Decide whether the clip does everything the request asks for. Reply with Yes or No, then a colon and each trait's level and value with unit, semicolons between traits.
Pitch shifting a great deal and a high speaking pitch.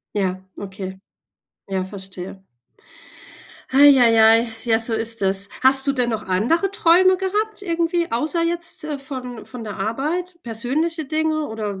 Yes: wide, 7.6 semitones; very high, 250 Hz